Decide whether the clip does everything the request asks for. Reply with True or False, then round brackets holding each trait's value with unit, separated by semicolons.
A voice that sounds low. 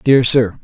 True (120 Hz)